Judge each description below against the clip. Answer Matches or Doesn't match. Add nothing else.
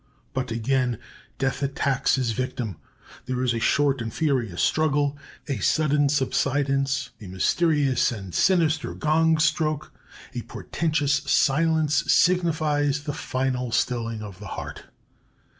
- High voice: Doesn't match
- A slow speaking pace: Matches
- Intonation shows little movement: Doesn't match